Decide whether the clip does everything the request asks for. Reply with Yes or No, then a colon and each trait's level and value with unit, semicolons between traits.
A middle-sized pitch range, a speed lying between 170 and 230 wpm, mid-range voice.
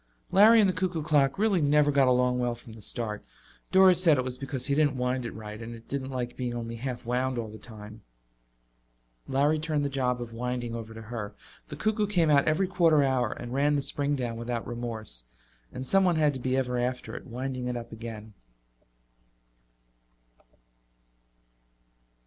No: average, 3.8 semitones; average, 185 wpm; low, 130 Hz